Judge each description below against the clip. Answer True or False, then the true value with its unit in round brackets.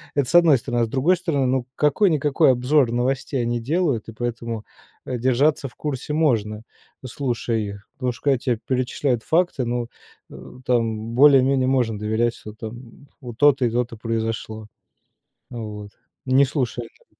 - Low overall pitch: True (125 Hz)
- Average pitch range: True (3.2 semitones)